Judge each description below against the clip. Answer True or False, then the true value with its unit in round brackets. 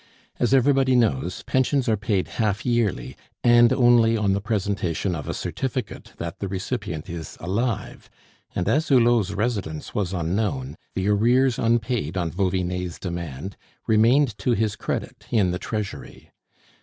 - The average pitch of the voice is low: True (105 Hz)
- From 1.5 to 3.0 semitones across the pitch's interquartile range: False (4.7 semitones)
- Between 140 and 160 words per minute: True (145 wpm)